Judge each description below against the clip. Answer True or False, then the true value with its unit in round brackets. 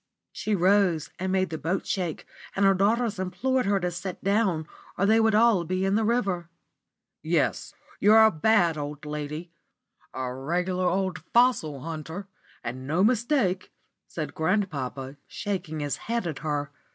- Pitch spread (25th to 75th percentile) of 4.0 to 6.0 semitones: True (4.7 semitones)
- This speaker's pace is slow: False (155 wpm)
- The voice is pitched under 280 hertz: True (185 Hz)